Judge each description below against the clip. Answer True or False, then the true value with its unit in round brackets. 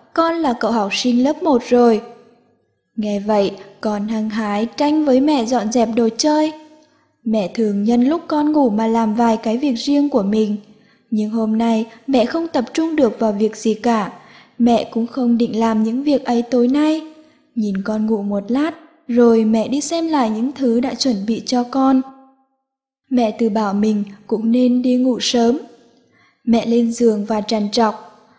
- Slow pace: False (185 wpm)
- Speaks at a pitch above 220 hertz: True (235 Hz)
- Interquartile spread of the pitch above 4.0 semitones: False (3.4 semitones)